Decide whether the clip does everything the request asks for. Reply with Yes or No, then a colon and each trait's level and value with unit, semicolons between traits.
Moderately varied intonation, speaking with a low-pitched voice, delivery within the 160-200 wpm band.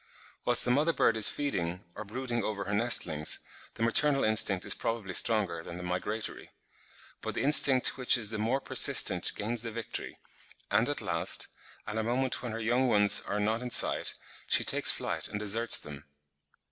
Yes: average, 3.2 semitones; low, 110 Hz; average, 185 wpm